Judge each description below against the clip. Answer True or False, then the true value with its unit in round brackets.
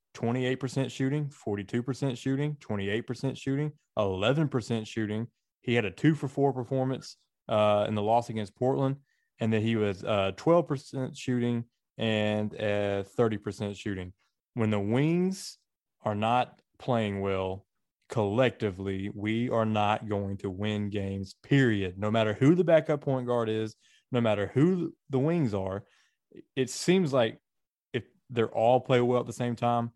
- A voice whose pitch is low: True (120 Hz)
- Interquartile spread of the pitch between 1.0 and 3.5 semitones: False (4.3 semitones)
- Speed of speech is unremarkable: True (150 wpm)